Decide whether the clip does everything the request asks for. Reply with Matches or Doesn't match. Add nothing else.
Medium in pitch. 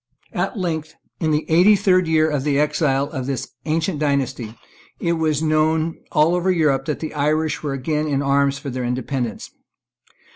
Matches